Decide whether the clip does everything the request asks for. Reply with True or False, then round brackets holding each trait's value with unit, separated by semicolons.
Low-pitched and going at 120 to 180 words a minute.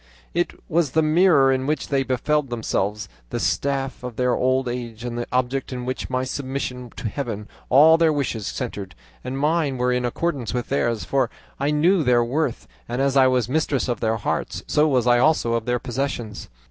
False (130 Hz; 200 wpm)